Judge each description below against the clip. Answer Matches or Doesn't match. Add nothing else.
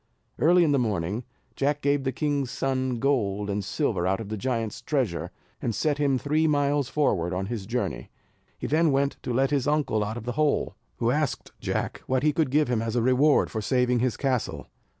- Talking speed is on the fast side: Matches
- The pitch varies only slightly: Doesn't match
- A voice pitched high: Doesn't match